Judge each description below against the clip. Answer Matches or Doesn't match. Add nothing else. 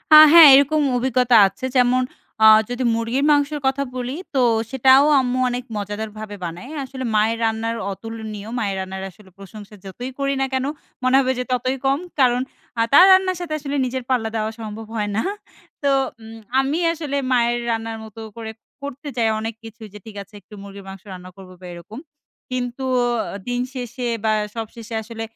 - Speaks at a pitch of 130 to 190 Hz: Doesn't match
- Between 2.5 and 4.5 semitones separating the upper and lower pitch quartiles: Matches